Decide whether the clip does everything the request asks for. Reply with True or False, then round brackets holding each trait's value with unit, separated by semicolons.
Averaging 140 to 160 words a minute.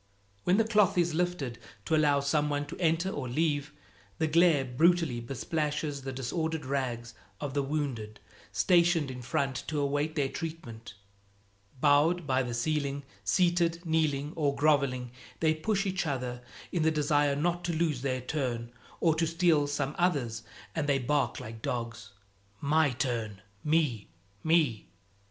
True (150 wpm)